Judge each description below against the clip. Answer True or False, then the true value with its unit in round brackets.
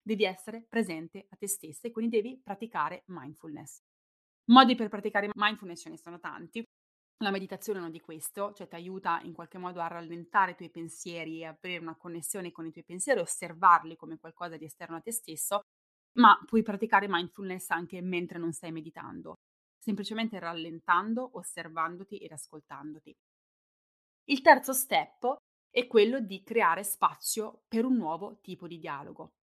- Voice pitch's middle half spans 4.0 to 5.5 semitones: True (4.3 semitones)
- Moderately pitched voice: True (180 Hz)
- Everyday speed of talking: True (160 wpm)